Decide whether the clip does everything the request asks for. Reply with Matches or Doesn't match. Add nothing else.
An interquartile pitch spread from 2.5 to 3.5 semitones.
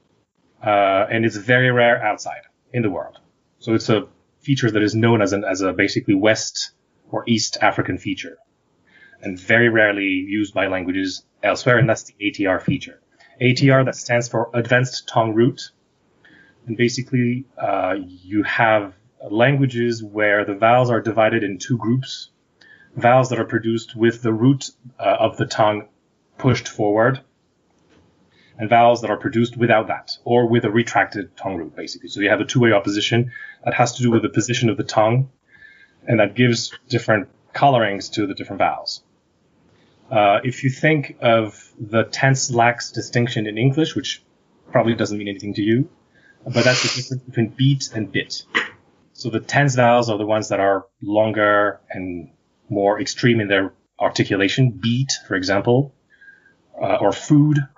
Matches